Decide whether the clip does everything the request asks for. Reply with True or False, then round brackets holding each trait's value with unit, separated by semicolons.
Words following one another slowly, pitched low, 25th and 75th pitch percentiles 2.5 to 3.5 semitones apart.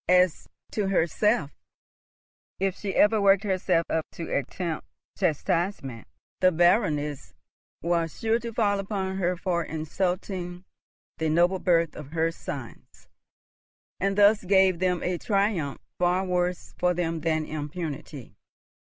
False (125 wpm; 180 Hz; 3.0 semitones)